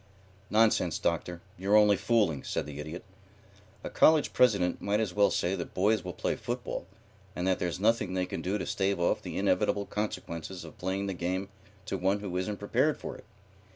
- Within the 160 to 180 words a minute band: No, average, 190 wpm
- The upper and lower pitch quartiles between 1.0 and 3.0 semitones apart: Yes, average, 2.7 semitones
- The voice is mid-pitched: No, very low, 95 Hz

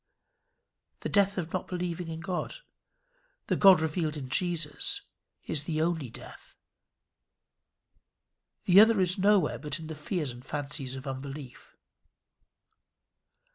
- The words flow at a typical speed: No, slow, 125 wpm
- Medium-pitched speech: Yes, medium, 160 Hz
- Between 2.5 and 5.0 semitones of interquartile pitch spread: Yes, average, 4.0 semitones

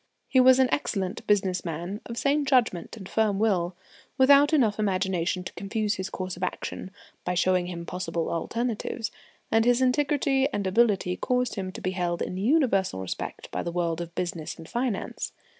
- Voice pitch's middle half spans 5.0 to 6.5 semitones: Yes, average, 5.3 semitones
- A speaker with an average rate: Yes, average, 175 wpm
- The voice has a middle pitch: No, high, 195 Hz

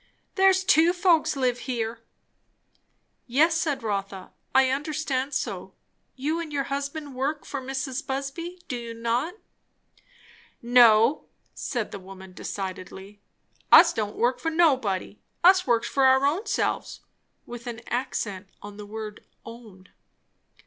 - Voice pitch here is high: Yes, very high, 255 Hz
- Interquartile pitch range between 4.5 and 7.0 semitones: Yes, average, 5.1 semitones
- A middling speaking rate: No, slow, 130 wpm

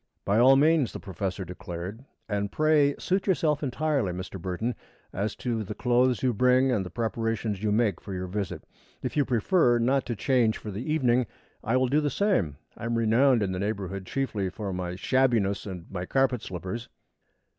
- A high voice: No, low, 115 Hz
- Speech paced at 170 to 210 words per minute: Yes, average, 190 wpm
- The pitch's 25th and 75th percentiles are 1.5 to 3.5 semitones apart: No, average, 5.1 semitones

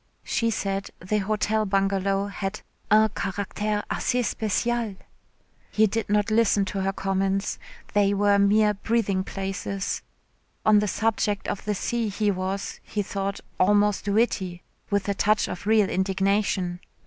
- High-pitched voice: Yes, high, 200 Hz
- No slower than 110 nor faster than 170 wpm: Yes, average, 140 wpm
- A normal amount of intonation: No, narrow, 1.5 semitones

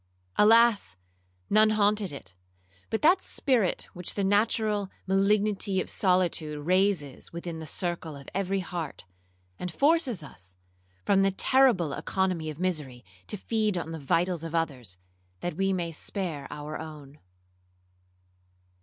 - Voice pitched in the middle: Yes, medium, 180 Hz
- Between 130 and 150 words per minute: Yes, slow, 135 wpm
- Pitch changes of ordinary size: Yes, average, 4.7 semitones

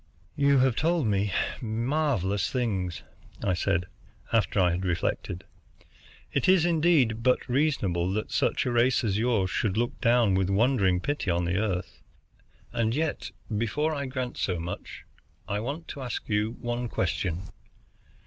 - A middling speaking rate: Yes, average, 150 wpm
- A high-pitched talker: No, low, 115 Hz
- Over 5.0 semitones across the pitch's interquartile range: Yes, wide, 5.4 semitones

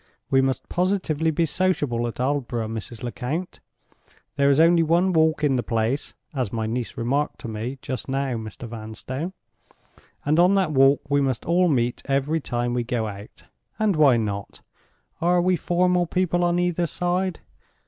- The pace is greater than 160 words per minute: Yes, average, 170 wpm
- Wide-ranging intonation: Yes, wide, 6.3 semitones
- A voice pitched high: No, medium, 140 Hz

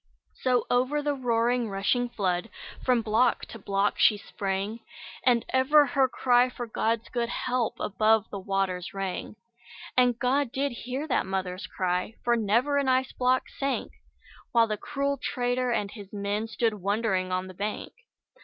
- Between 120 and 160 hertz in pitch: No, high, 230 Hz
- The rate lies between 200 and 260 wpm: No, average, 160 wpm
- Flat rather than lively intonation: No, average, 4.0 semitones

